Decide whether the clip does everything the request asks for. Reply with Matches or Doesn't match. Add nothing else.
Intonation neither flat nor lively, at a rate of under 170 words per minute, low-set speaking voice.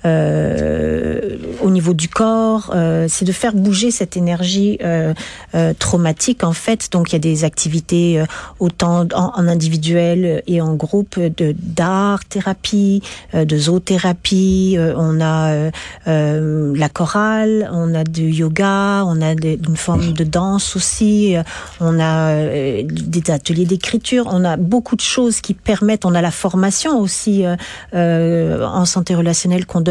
Doesn't match